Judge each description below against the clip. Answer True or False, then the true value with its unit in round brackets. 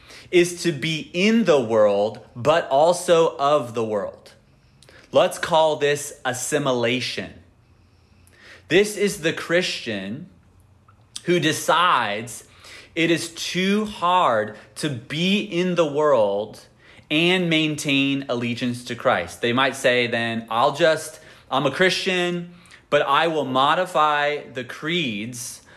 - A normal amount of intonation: False (6.8 semitones)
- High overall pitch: False (140 Hz)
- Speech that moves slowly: True (115 wpm)